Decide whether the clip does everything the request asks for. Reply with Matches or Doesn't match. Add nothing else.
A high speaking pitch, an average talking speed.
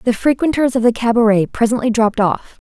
Matches